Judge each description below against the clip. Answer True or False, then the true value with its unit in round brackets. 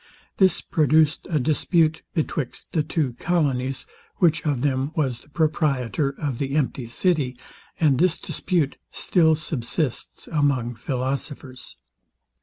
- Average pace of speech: False (120 wpm)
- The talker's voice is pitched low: False (145 Hz)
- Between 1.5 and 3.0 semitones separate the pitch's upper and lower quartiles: False (3.4 semitones)